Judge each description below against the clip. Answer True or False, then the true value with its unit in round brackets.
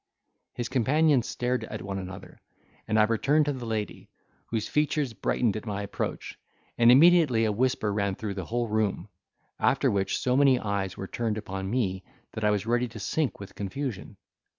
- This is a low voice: True (110 Hz)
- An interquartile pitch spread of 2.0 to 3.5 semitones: False (4.1 semitones)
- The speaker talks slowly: False (180 wpm)